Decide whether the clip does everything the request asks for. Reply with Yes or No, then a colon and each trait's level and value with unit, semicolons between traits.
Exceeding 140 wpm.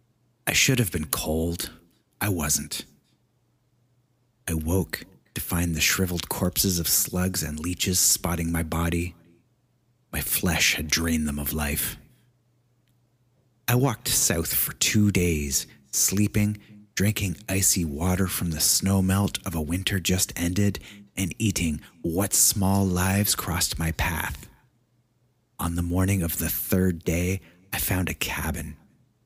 No: slow, 135 wpm